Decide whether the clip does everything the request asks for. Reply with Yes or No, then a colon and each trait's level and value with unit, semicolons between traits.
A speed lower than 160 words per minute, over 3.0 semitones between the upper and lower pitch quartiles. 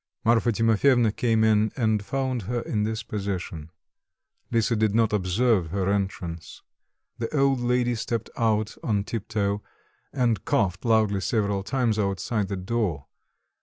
No: average, 140 wpm; average, 2.7 semitones